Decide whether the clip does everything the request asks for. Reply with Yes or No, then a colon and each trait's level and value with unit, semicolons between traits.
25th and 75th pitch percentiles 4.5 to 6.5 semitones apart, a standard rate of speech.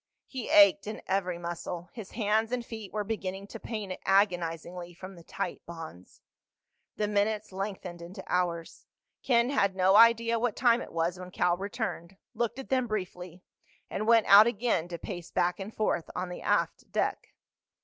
No: average, 4.0 semitones; average, 170 wpm